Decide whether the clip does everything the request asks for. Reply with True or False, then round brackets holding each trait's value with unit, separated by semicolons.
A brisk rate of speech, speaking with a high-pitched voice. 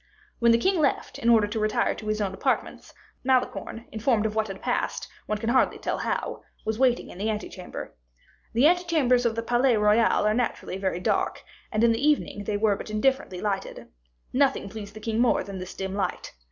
True (210 wpm; 220 Hz)